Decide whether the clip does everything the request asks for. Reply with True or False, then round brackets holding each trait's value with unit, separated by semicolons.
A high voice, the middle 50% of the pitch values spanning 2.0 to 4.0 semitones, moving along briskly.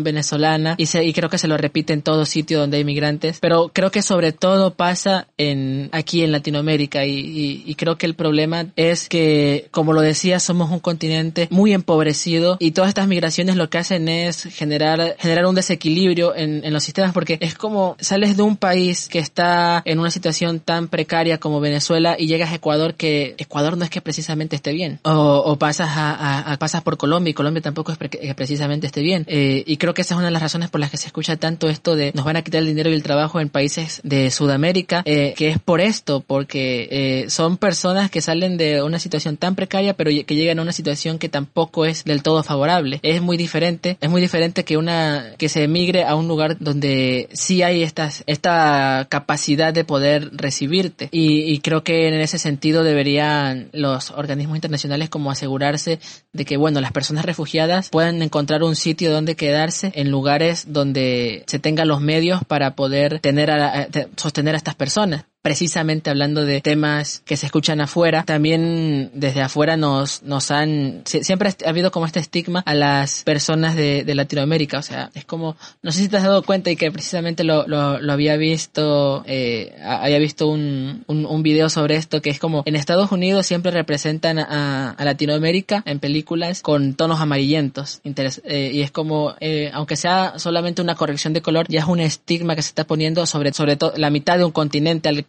False (155 Hz; 2.4 semitones; 205 wpm)